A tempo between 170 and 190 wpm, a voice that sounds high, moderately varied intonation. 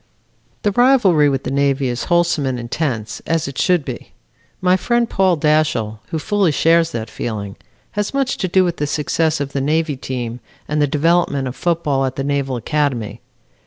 No: average, 185 wpm; medium, 150 Hz; average, 4.6 semitones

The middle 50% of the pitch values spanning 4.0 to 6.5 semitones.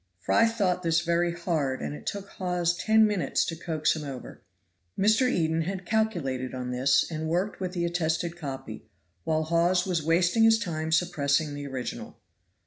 No: average, 3.2 semitones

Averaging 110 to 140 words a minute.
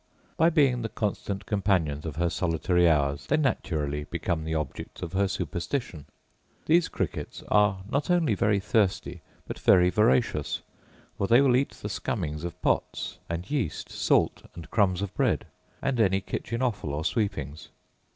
No: average, 160 wpm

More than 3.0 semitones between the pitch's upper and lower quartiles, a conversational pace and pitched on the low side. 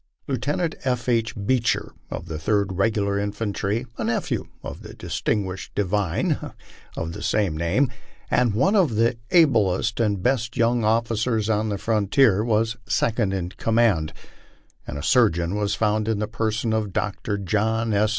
No: narrow, 2.5 semitones; average, 155 wpm; low, 110 Hz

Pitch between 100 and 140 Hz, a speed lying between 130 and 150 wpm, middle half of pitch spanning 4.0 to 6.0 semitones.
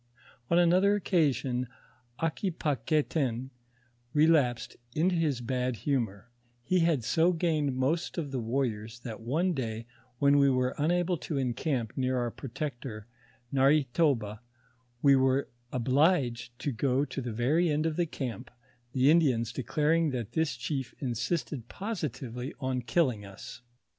Yes: low, 135 Hz; slow, 135 wpm; average, 4.6 semitones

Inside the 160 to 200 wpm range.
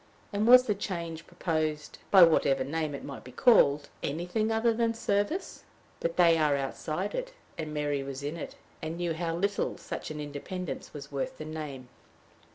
Yes: average, 175 wpm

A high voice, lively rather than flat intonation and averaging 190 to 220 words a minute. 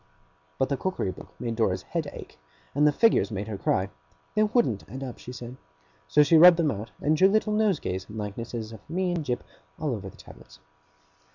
No: low, 130 Hz; wide, 8.0 semitones; fast, 205 wpm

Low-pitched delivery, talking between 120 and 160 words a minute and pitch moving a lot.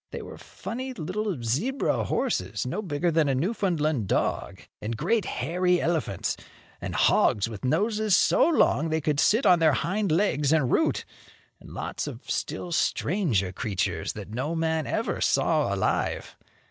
No: medium, 160 Hz; average, 155 wpm; wide, 7.4 semitones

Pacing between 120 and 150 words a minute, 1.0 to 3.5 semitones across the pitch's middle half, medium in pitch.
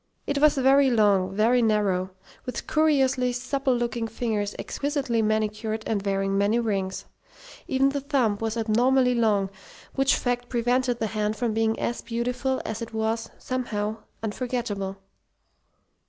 No: average, 140 wpm; average, 3.1 semitones; high, 230 Hz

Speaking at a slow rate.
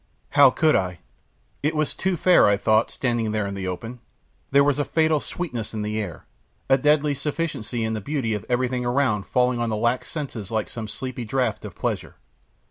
No: average, 200 wpm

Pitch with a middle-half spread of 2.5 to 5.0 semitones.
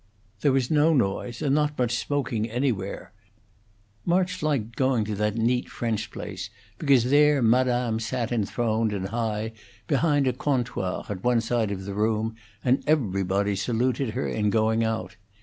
Yes: average, 3.6 semitones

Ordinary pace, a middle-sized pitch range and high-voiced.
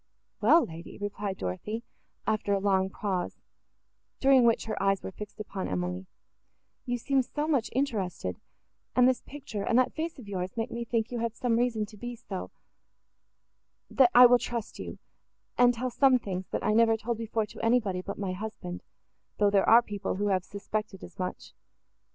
Yes: average, 175 wpm; average, 3.8 semitones; high, 215 Hz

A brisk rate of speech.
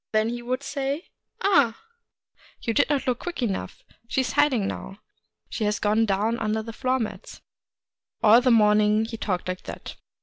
No: average, 190 wpm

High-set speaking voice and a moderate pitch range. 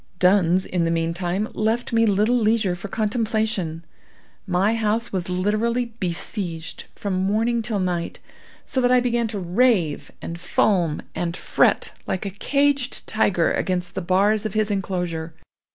Yes: high, 200 Hz; average, 4.0 semitones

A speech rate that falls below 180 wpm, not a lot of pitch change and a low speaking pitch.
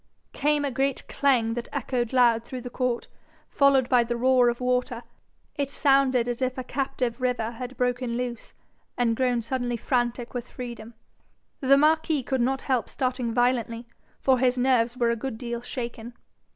No: average, 170 wpm; narrow, 1.7 semitones; very high, 250 Hz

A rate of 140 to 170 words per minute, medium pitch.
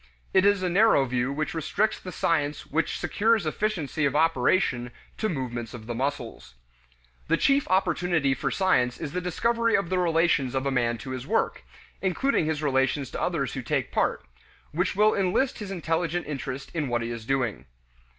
No: average, 180 wpm; medium, 155 Hz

